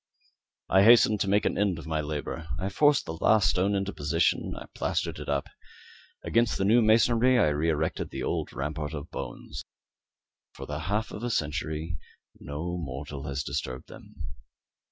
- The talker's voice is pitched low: Yes, very low, 85 Hz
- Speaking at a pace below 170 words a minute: No, average, 175 wpm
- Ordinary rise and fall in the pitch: No, wide, 5.8 semitones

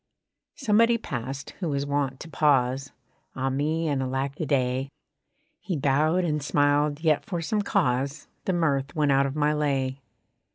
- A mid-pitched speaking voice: Yes, medium, 145 Hz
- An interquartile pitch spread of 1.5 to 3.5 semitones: Yes, average, 2.7 semitones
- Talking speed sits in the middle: Yes, average, 160 wpm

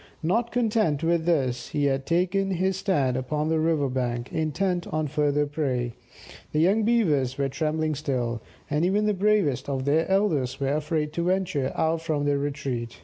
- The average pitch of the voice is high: No, medium, 155 Hz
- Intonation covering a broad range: No, average, 4.4 semitones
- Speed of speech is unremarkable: Yes, average, 175 wpm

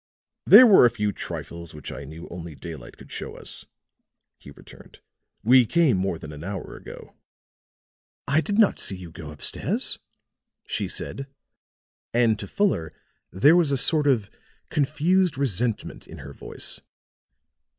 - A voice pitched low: Yes, low, 110 Hz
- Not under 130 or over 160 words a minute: Yes, average, 150 wpm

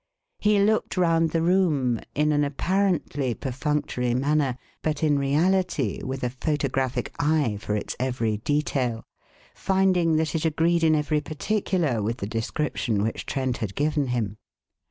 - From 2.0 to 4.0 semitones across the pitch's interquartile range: No, average, 4.7 semitones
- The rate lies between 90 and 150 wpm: Yes, average, 145 wpm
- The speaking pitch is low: No, medium, 145 Hz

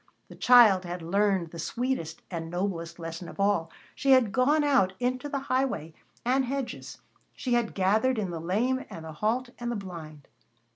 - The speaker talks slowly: No, average, 180 wpm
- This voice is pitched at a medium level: No, high, 205 Hz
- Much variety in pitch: Yes, wide, 7.1 semitones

